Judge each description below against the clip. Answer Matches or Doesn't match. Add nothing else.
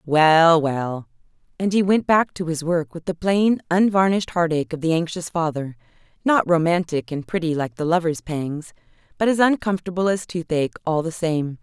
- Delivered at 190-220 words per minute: Doesn't match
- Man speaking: Doesn't match